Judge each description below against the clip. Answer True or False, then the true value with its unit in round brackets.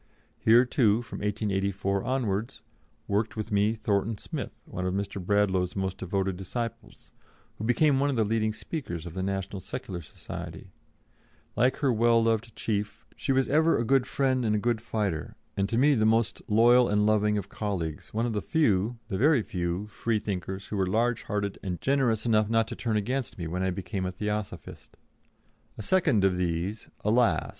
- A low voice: True (105 Hz)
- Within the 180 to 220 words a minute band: True (185 wpm)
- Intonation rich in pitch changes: False (3.3 semitones)